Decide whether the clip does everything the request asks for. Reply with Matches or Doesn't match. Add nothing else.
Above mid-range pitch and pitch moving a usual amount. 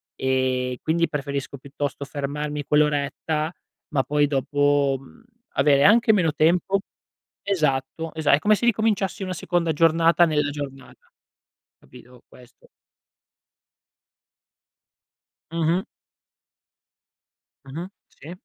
Doesn't match